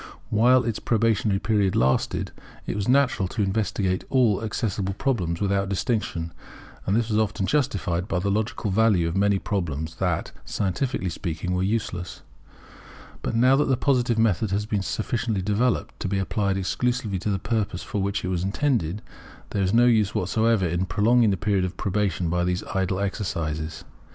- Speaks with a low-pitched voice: Yes, low, 100 Hz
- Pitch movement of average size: Yes, average, 3.4 semitones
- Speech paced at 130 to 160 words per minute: No, average, 170 wpm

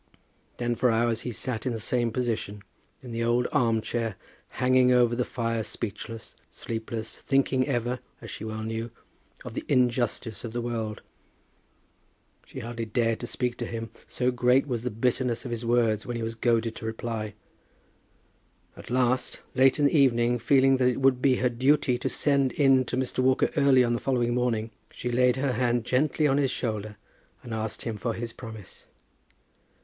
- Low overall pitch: Yes, low, 120 Hz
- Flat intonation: Yes, narrow, 1.9 semitones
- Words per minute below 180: No, average, 185 wpm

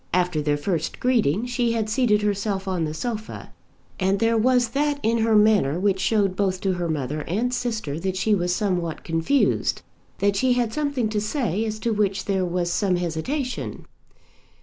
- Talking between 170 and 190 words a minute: Yes, average, 180 wpm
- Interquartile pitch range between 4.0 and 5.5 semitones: Yes, average, 4.4 semitones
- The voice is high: Yes, high, 205 Hz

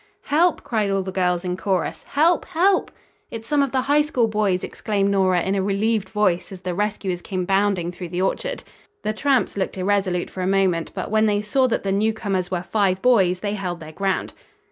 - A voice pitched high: Yes, high, 195 Hz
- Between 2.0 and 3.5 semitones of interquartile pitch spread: Yes, average, 3.1 semitones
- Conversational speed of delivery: No, fast, 210 wpm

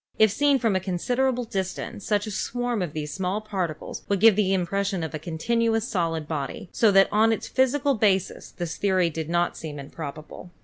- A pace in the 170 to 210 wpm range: Yes, average, 190 wpm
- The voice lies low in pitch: No, high, 195 Hz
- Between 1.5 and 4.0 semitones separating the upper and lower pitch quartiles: No, average, 4.9 semitones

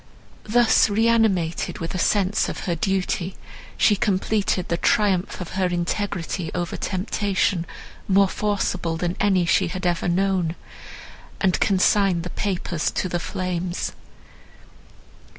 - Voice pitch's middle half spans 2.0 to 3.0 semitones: Yes, narrow, 2.4 semitones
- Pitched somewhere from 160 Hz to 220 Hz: Yes, medium, 185 Hz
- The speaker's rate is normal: No, slow, 125 wpm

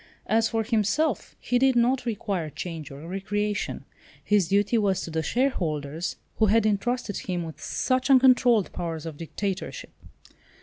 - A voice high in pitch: Yes, high, 205 Hz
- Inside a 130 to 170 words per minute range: Yes, average, 145 wpm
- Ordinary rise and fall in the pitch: No, wide, 5.7 semitones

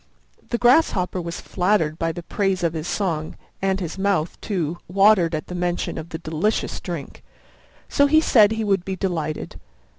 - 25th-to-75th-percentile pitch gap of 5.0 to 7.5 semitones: No, average, 3.4 semitones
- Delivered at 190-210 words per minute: No, average, 175 wpm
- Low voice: No, medium, 180 Hz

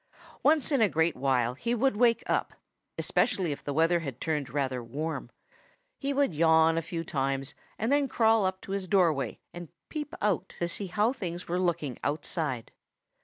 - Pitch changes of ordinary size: No, wide, 6.4 semitones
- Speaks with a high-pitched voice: No, medium, 170 Hz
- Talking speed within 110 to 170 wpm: No, average, 180 wpm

